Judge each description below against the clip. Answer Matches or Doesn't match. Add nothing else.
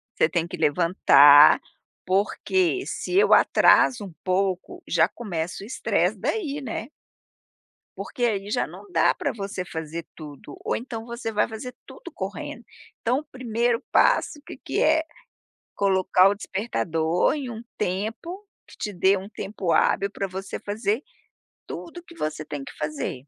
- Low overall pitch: Doesn't match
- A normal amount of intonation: Doesn't match